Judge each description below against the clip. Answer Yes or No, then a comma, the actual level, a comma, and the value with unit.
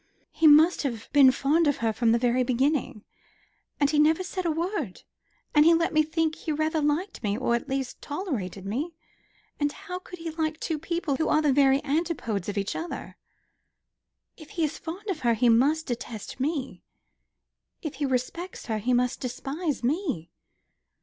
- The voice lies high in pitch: Yes, very high, 290 Hz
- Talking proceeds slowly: No, average, 185 wpm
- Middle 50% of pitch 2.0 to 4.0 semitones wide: No, average, 4.6 semitones